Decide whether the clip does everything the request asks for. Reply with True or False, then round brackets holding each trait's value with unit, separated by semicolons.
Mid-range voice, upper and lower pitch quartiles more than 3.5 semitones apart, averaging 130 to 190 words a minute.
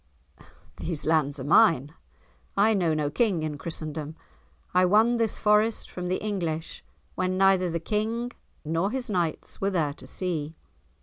True (180 Hz; 5.1 semitones; 150 wpm)